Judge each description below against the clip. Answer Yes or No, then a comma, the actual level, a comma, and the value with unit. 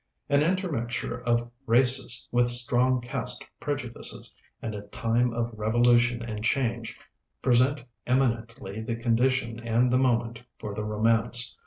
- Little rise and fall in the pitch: Yes, narrow, 1.6 semitones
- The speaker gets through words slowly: Yes, slow, 130 wpm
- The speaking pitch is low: Yes, low, 120 Hz